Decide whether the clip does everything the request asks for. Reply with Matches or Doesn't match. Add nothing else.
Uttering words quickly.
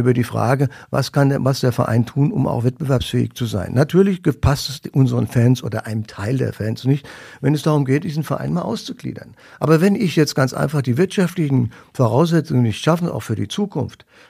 Matches